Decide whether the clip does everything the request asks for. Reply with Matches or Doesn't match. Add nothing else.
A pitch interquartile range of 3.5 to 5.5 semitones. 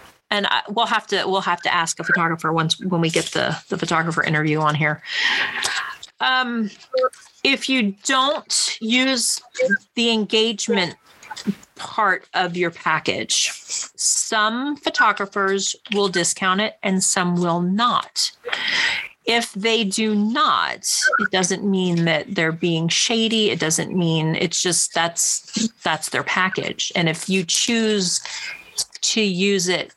Matches